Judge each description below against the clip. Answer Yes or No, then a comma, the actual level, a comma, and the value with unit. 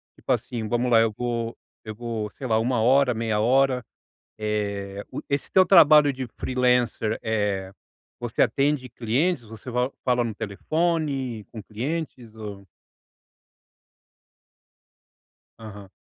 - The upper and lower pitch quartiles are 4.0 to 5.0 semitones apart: No, average, 3.4 semitones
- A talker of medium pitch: No, low, 120 Hz